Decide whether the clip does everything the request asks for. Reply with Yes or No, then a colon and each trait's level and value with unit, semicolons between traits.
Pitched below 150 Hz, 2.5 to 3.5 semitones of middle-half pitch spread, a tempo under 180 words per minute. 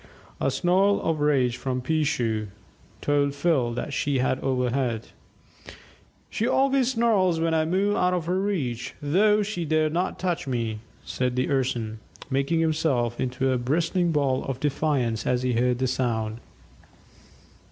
No: medium, 140 Hz; average, 5.3 semitones; average, 150 wpm